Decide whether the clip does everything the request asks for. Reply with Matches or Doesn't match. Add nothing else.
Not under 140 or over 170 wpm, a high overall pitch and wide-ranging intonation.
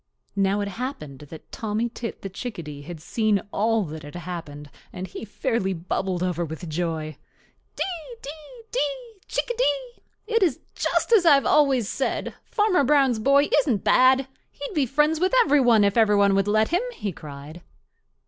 Matches